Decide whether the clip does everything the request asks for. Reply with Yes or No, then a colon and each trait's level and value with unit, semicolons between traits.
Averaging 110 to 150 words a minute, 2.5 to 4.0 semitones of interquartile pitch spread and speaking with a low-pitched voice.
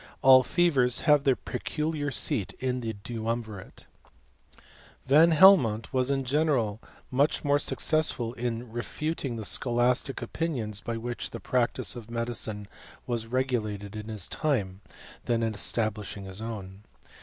Yes: average, 140 wpm; average, 3.7 semitones; low, 120 Hz